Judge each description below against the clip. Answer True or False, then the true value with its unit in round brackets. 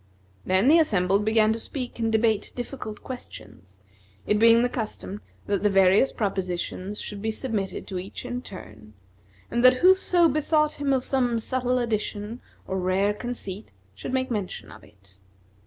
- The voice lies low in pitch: False (220 Hz)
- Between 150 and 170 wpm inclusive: True (160 wpm)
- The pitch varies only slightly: False (4.6 semitones)